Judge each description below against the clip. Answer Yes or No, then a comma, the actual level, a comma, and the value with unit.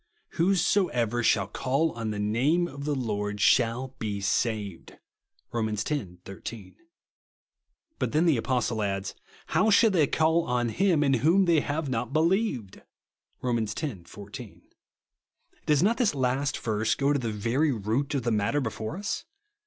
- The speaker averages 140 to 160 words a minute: Yes, average, 155 wpm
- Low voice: Yes, low, 125 Hz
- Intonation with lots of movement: Yes, wide, 5.9 semitones